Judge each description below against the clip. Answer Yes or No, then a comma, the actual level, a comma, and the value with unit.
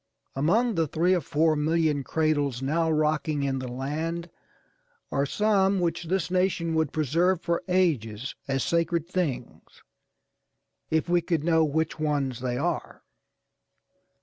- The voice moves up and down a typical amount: Yes, average, 3.1 semitones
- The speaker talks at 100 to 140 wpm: Yes, slow, 135 wpm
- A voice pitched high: No, medium, 160 Hz